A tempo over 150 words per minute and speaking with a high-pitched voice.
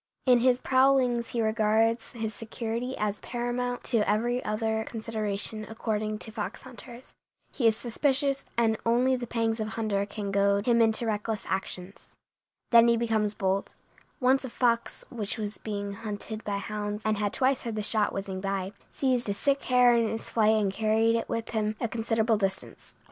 Yes: average, 175 wpm; high, 225 Hz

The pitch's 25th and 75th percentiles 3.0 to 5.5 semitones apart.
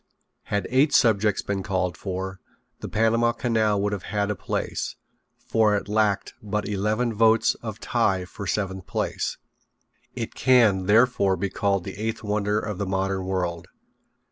No: narrow, 2.5 semitones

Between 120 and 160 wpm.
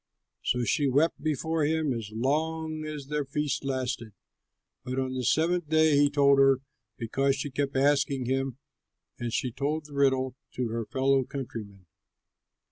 Yes: average, 155 wpm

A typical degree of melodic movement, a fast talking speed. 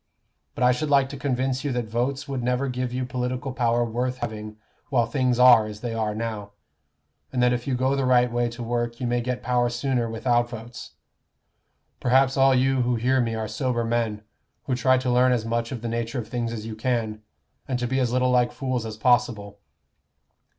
No: narrow, 1.7 semitones; fast, 215 wpm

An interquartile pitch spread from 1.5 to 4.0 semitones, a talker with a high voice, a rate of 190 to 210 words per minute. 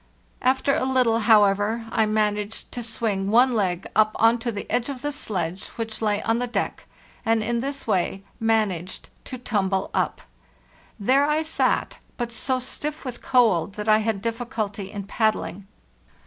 No: average, 3.2 semitones; high, 225 Hz; average, 165 wpm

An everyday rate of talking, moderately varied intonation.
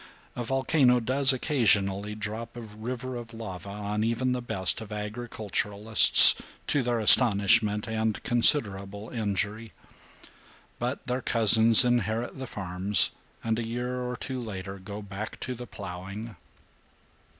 No: slow, 130 wpm; average, 3.0 semitones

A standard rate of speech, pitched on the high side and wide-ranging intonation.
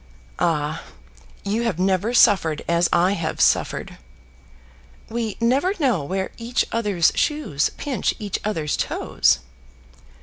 No: slow, 115 wpm; high, 195 Hz; wide, 5.8 semitones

